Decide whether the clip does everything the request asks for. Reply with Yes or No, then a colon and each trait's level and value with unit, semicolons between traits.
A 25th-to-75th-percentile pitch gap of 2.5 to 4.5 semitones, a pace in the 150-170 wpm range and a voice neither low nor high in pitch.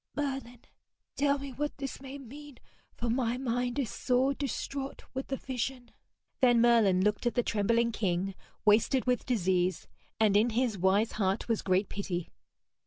No: average, 4.2 semitones; average, 160 wpm; high, 240 Hz